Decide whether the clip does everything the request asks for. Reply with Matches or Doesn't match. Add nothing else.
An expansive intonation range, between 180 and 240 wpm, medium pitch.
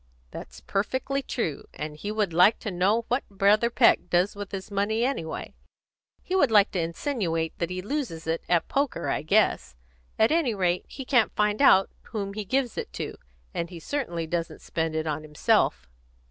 Doesn't match